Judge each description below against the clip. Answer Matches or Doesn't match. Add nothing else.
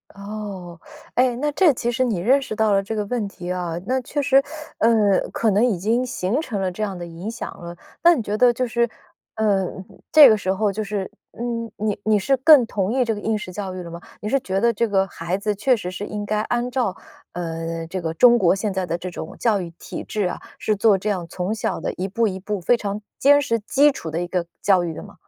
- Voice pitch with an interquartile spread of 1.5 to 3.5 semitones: Doesn't match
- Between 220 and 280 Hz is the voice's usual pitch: Doesn't match